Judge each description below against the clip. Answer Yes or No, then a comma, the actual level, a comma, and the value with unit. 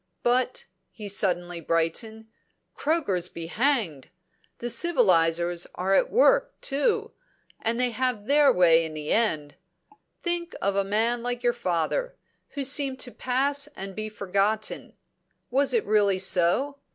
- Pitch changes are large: Yes, wide, 6.8 semitones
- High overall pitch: Yes, high, 220 Hz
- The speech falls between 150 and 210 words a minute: No, average, 140 wpm